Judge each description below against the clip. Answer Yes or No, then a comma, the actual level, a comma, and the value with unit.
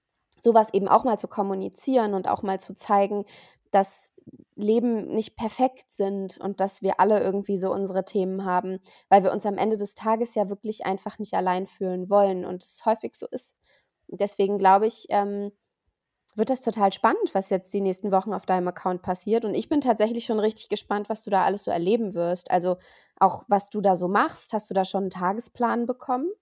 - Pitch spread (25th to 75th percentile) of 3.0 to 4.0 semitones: No, narrow, 2.4 semitones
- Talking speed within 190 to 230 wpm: Yes, average, 200 wpm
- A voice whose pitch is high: Yes, high, 200 Hz